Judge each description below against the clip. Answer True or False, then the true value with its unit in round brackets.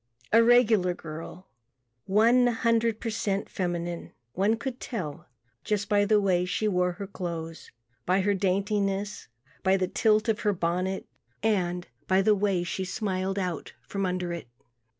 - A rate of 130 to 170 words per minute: True (150 wpm)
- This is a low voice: False (195 Hz)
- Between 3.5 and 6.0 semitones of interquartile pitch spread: False (2.9 semitones)